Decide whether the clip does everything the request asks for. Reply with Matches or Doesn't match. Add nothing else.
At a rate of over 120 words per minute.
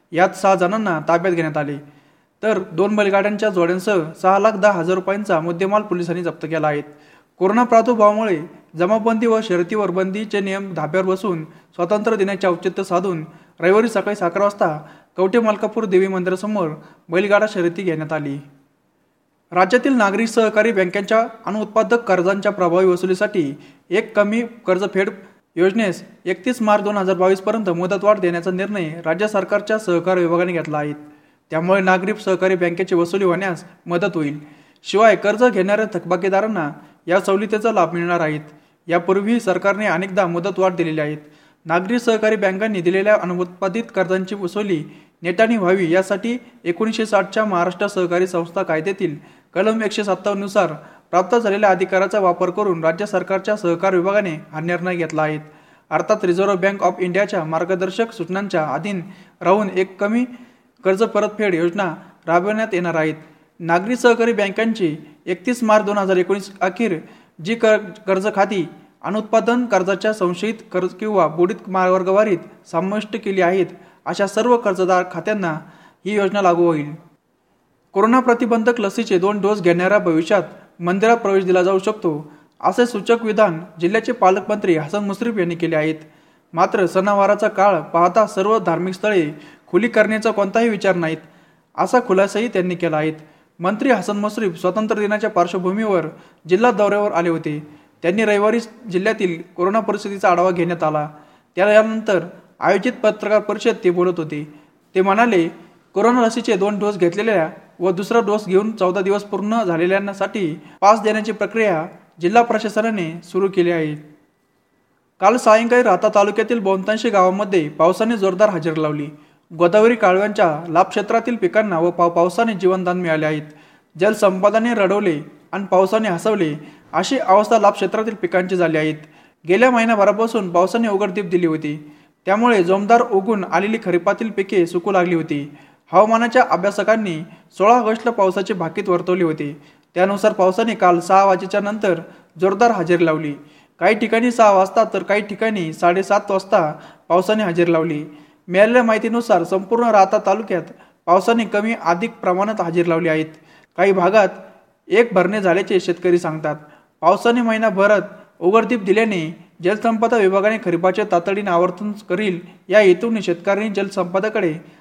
Matches